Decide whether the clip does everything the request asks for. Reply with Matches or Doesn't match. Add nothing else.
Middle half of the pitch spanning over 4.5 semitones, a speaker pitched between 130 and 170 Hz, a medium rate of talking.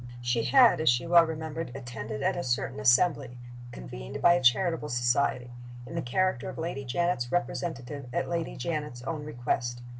Matches